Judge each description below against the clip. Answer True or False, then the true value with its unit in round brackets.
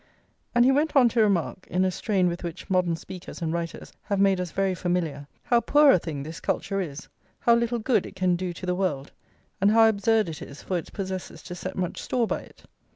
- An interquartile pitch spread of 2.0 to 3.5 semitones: False (4.2 semitones)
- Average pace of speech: False (230 wpm)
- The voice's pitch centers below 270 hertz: True (185 Hz)